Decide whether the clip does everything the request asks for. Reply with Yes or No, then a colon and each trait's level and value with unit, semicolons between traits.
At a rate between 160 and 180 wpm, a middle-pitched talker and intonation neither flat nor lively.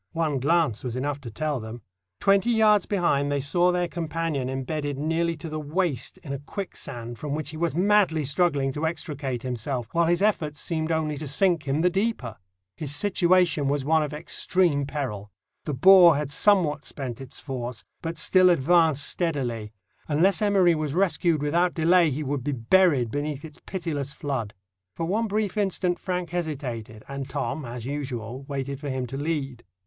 Yes: average, 175 wpm; medium, 150 Hz; average, 4.2 semitones